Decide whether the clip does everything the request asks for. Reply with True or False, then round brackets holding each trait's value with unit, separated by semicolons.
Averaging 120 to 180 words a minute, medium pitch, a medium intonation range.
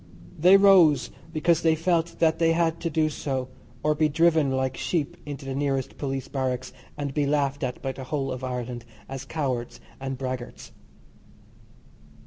True (165 wpm; 145 Hz; 3.4 semitones)